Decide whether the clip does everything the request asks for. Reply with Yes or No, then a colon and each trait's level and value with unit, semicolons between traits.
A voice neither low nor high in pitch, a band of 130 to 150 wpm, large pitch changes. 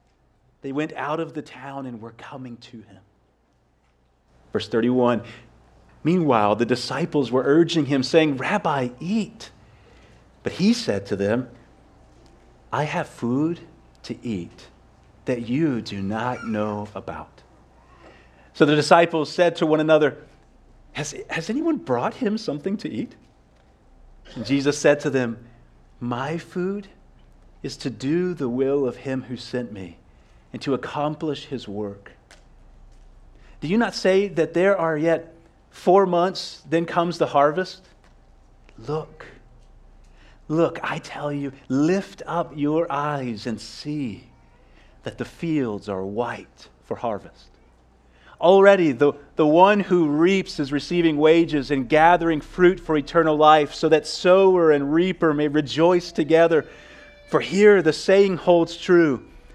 Yes: medium, 145 Hz; slow, 135 wpm; wide, 6.3 semitones